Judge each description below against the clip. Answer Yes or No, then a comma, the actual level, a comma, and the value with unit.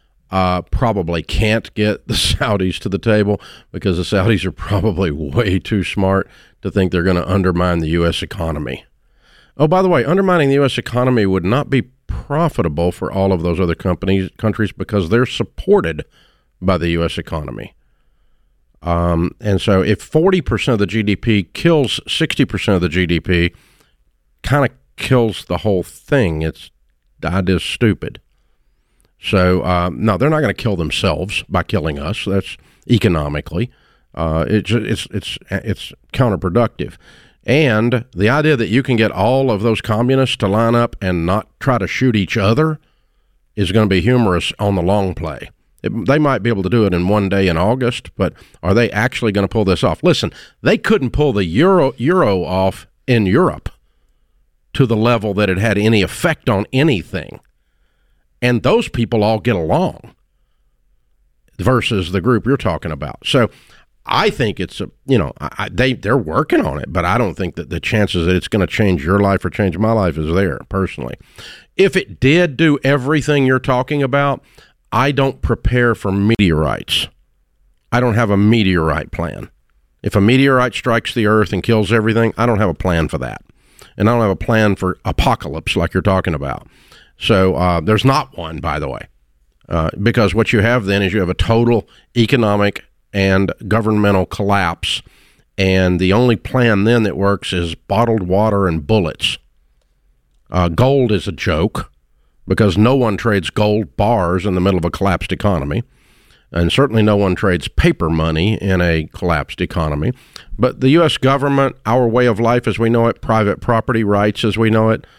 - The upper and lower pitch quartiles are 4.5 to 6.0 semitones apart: Yes, average, 4.8 semitones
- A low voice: Yes, low, 100 Hz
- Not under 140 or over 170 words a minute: No, average, 180 wpm